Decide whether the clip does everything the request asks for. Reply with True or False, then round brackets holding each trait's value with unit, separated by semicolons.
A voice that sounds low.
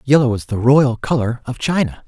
True (125 Hz)